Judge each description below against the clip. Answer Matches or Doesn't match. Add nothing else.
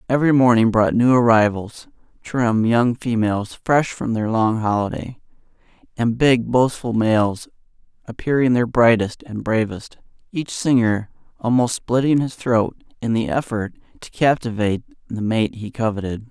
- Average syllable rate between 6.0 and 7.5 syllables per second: Doesn't match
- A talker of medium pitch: Doesn't match